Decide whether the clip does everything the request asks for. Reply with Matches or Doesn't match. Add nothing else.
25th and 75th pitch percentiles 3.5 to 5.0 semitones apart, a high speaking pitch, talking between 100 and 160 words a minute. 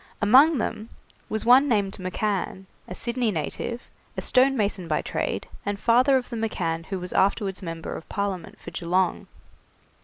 Matches